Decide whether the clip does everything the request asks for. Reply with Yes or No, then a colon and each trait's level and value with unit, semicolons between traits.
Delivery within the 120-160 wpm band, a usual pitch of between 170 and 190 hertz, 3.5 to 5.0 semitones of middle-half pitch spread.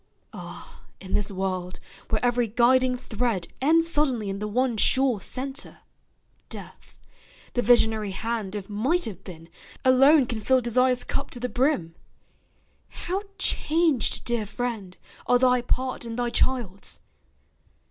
No: slow, 135 wpm; high, 240 Hz; average, 3.8 semitones